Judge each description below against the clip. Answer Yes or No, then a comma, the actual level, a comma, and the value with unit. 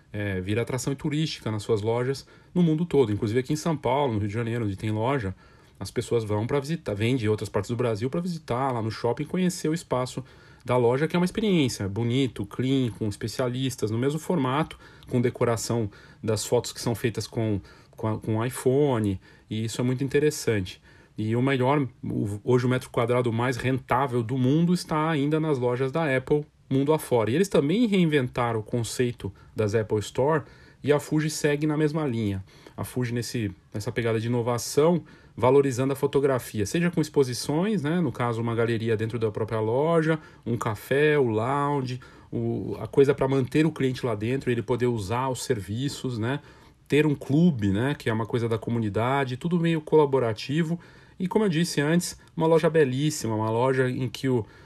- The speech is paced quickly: Yes, fast, 195 wpm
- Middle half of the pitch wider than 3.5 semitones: Yes, average, 4.5 semitones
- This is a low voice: Yes, low, 125 Hz